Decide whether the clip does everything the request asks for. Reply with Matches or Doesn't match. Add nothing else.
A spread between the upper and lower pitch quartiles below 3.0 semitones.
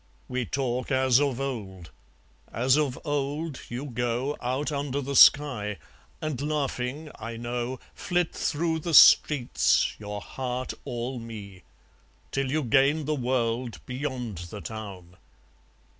Doesn't match